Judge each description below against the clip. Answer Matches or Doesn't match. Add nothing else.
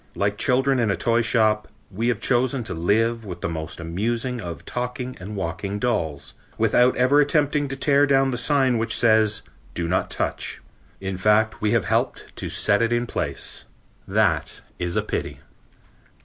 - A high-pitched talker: Doesn't match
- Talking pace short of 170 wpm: Doesn't match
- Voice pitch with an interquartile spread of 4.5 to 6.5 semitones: Doesn't match